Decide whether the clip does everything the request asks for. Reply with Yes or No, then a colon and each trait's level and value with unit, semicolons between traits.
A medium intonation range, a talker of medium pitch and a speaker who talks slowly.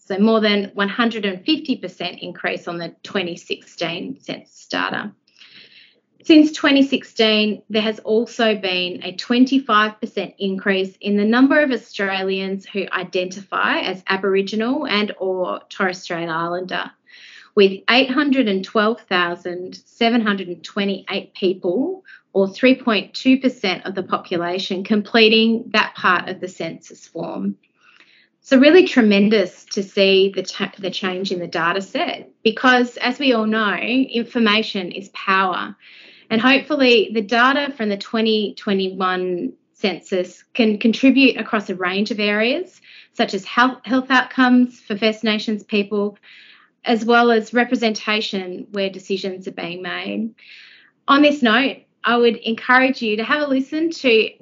No: average, 4.0 semitones; high, 215 Hz; slow, 125 wpm